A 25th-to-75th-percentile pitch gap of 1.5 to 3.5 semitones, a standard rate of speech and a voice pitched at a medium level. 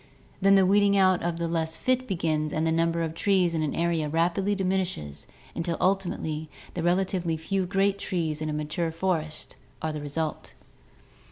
Yes: average, 3.2 semitones; average, 180 wpm; medium, 170 Hz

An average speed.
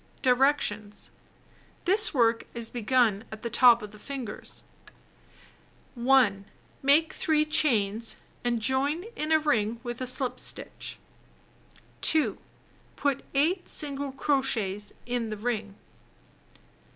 No: slow, 115 wpm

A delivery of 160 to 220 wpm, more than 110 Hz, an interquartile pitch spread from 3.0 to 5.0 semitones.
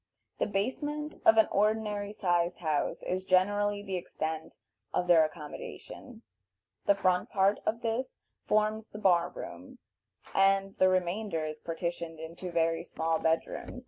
No: average, 145 wpm; medium, 185 Hz; average, 3.9 semitones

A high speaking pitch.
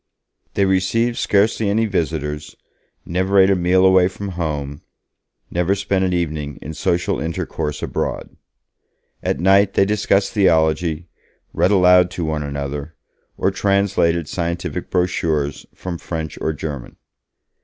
No: very low, 90 Hz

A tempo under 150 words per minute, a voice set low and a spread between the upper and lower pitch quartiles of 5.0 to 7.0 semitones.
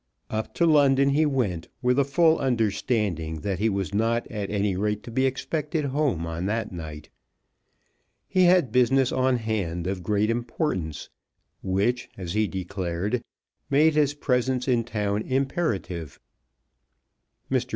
Yes: average, 140 wpm; low, 115 Hz; wide, 5.6 semitones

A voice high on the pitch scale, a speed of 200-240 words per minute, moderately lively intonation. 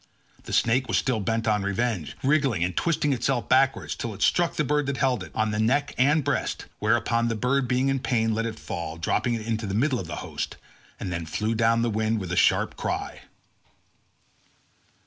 No: low, 115 Hz; fast, 205 wpm; average, 3.5 semitones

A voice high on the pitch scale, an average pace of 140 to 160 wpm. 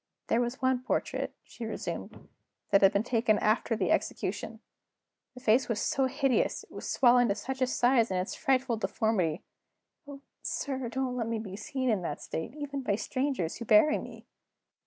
No: high, 240 Hz; average, 185 wpm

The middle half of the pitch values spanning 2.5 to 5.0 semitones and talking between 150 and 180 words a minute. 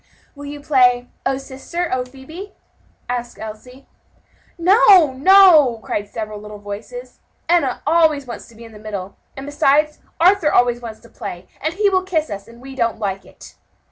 No: wide, 5.6 semitones; average, 170 wpm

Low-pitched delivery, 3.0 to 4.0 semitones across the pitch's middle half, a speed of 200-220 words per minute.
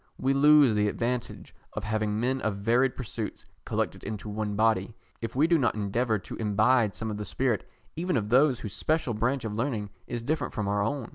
Yes: low, 115 Hz; average, 3.6 semitones; fast, 205 wpm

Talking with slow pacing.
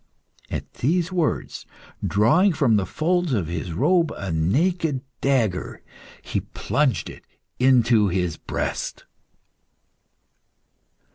Yes: slow, 100 wpm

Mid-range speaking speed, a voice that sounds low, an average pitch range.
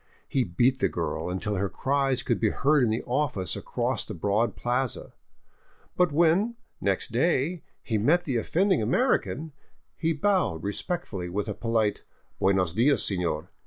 No: average, 160 wpm; low, 120 Hz; wide, 7.4 semitones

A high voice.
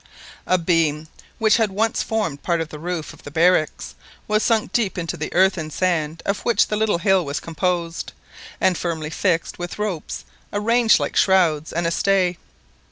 No: medium, 180 Hz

